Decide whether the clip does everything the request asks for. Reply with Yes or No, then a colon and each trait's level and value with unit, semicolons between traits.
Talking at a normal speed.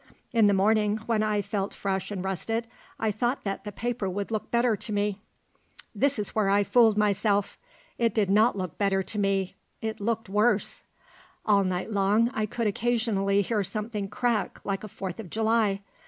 Yes: average, 185 wpm